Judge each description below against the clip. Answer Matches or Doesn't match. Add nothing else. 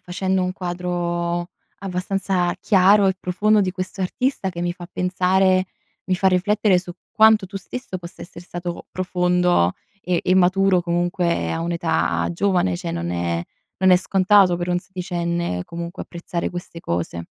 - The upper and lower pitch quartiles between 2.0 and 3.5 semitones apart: Doesn't match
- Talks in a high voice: Doesn't match